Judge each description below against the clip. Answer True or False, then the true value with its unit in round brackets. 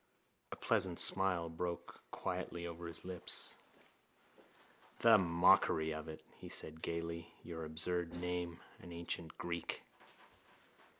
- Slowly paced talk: True (115 wpm)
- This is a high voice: False (85 Hz)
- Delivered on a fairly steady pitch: True (1.2 semitones)